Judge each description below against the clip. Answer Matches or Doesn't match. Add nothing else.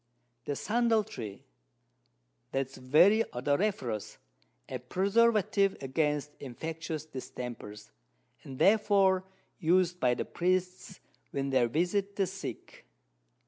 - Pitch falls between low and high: Matches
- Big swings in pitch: Matches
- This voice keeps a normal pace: Doesn't match